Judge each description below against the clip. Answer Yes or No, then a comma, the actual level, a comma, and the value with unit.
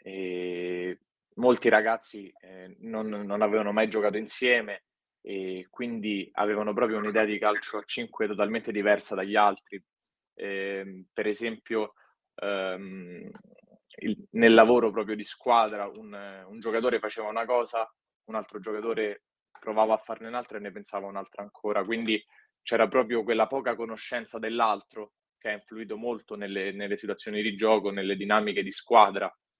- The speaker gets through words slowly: No, average, 145 wpm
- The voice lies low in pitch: Yes, low, 105 Hz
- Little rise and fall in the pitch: Yes, narrow, 2.1 semitones